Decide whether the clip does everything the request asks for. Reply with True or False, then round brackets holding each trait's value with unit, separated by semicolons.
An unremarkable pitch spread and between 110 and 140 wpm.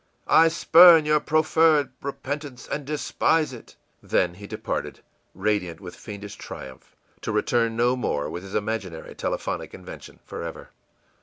False (7.2 semitones; 135 wpm)